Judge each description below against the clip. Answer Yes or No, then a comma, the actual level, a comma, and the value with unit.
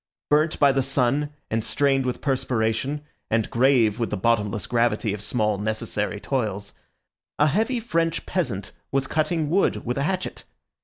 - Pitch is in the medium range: No, low, 125 Hz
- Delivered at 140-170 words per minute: Yes, average, 155 wpm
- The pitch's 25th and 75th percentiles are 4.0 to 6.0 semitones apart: Yes, average, 5.2 semitones